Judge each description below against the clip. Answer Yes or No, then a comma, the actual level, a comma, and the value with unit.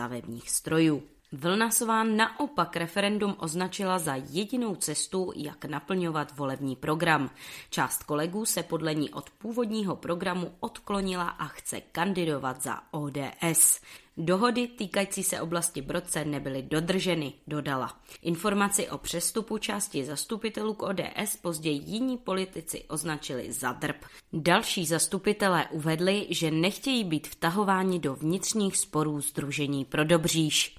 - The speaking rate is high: No, average, 120 wpm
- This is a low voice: No, medium, 170 Hz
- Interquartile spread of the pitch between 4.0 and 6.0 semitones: Yes, average, 4.7 semitones